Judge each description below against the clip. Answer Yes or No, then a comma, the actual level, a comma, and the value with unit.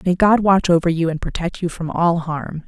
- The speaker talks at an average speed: No, fast, 245 wpm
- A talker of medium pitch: Yes, medium, 170 Hz